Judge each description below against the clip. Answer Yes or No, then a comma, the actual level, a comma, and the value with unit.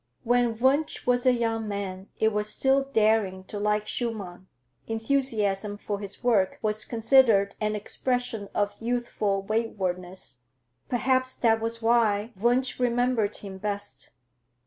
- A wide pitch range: No, average, 3.1 semitones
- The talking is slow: Yes, slow, 130 wpm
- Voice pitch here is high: Yes, high, 220 Hz